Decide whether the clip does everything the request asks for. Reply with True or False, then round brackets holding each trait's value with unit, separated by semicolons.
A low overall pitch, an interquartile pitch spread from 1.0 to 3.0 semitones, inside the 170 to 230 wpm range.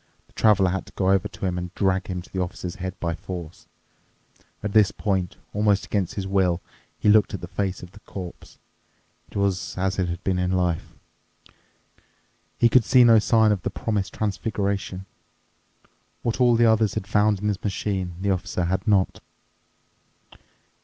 True (95 Hz; 2.4 semitones; 180 wpm)